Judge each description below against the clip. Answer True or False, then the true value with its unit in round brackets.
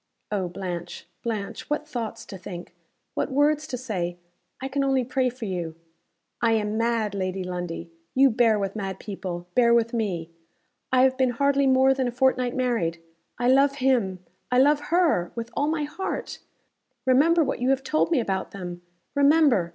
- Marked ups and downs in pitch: True (5.8 semitones)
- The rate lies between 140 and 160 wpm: False (175 wpm)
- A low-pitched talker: False (240 Hz)